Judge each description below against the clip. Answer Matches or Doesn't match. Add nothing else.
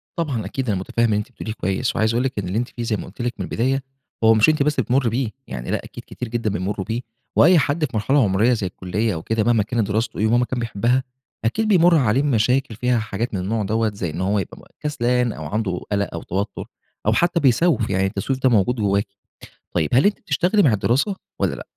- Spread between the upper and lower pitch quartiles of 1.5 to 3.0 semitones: Doesn't match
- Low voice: Matches